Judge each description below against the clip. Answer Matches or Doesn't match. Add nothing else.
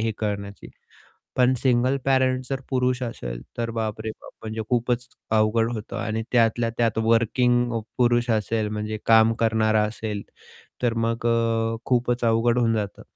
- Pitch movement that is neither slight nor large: Doesn't match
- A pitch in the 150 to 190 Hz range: Doesn't match